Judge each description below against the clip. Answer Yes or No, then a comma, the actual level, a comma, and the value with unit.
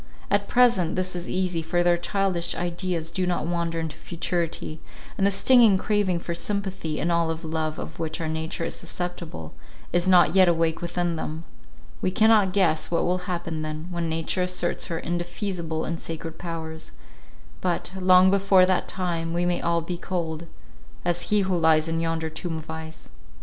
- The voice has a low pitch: No, medium, 175 Hz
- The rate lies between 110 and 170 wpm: No, average, 180 wpm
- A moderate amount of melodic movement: No, narrow, 2.0 semitones